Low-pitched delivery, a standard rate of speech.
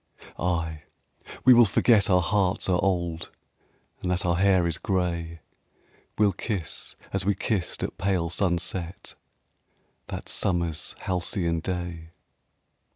No: very low, 90 Hz; slow, 120 wpm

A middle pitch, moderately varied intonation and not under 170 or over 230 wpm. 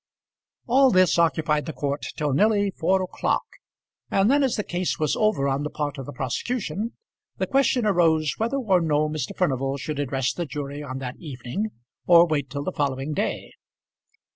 No: medium, 155 Hz; wide, 5.7 semitones; average, 180 wpm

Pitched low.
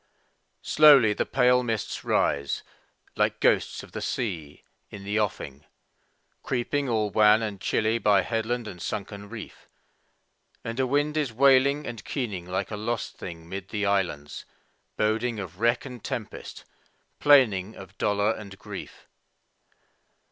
Yes: low, 110 Hz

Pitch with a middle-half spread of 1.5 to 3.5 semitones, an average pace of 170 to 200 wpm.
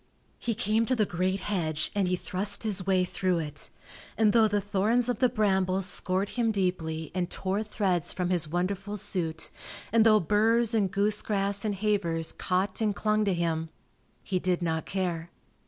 Yes: average, 2.9 semitones; average, 175 wpm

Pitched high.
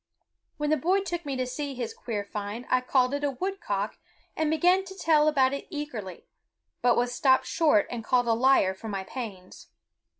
Yes: very high, 260 Hz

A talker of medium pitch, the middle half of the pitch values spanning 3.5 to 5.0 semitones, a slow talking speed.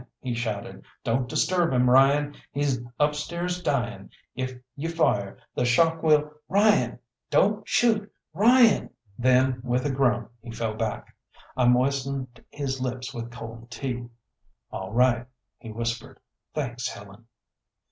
No: low, 130 Hz; average, 3.8 semitones; slow, 130 wpm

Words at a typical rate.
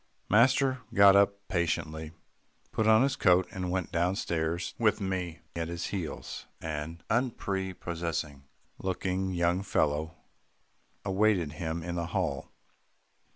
No: slow, 120 wpm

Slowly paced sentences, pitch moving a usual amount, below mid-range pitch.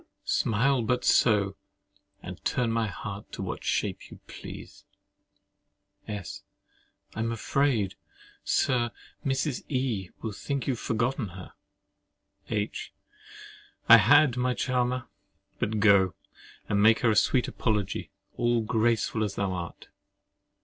Yes: slow, 125 wpm; average, 3.4 semitones; low, 115 Hz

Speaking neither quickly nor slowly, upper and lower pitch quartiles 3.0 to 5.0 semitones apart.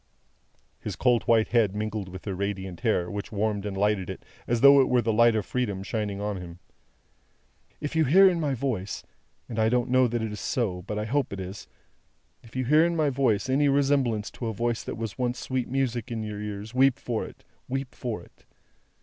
No: fast, 215 wpm; average, 3.9 semitones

